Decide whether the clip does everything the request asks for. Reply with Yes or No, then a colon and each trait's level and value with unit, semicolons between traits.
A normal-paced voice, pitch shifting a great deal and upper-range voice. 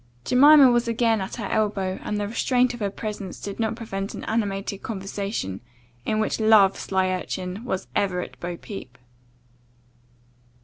No: average, 160 wpm; average, 3.0 semitones; high, 205 Hz